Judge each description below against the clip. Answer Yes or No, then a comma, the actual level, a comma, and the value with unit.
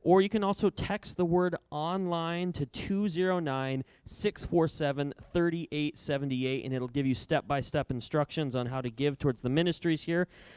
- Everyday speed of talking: Yes, average, 160 wpm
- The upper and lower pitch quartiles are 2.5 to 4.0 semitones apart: No, average, 4.6 semitones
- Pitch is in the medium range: Yes, medium, 150 Hz